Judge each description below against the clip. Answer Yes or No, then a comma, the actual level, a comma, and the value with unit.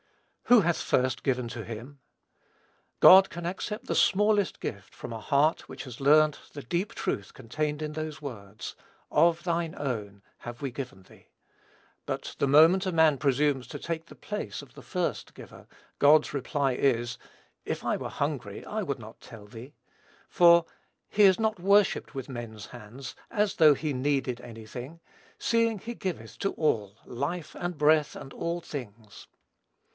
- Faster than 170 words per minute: No, average, 165 wpm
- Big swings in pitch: Yes, wide, 5.9 semitones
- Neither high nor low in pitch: Yes, medium, 145 Hz